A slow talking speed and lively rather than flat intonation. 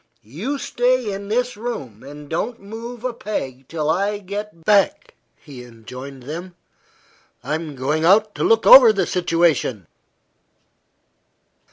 Yes: slow, 130 wpm; wide, 7.3 semitones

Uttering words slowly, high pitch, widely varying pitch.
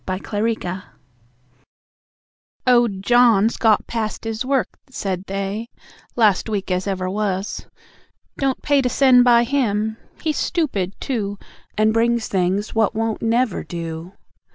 No: slow, 130 wpm; high, 220 Hz; average, 3.6 semitones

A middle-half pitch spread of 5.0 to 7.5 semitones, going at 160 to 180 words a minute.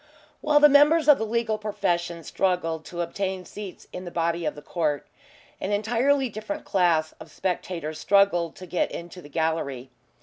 No: average, 4.6 semitones; average, 170 wpm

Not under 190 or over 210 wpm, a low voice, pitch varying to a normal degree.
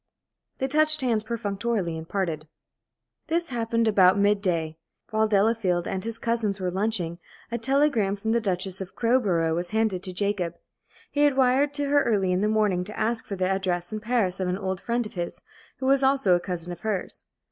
No: average, 200 wpm; high, 205 Hz; average, 4.2 semitones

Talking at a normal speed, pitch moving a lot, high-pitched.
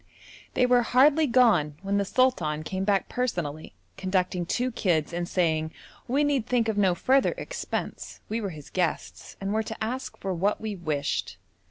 Yes: average, 175 wpm; wide, 6.1 semitones; high, 200 Hz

